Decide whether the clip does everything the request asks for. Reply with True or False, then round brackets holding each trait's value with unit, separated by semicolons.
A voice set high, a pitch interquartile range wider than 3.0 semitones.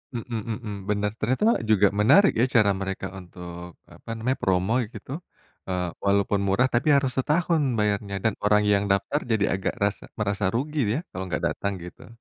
False (105 Hz; 3.9 semitones)